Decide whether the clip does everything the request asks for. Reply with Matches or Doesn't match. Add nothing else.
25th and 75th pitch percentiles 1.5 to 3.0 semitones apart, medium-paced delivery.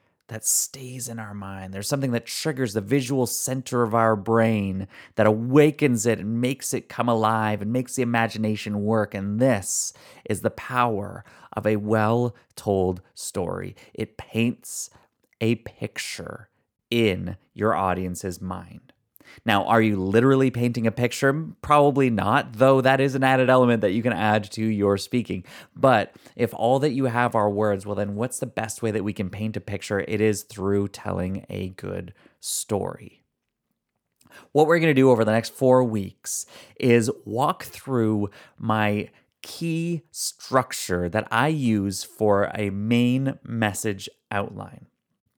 Doesn't match